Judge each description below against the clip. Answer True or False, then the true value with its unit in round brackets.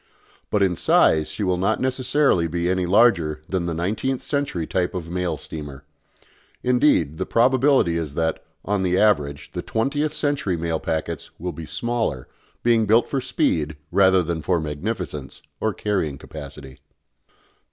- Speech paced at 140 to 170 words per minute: True (150 wpm)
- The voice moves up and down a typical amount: False (6.2 semitones)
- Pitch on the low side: True (90 Hz)